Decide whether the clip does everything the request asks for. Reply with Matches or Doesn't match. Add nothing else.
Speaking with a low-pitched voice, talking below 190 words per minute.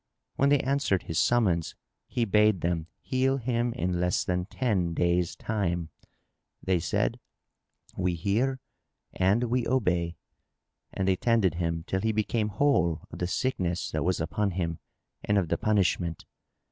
Matches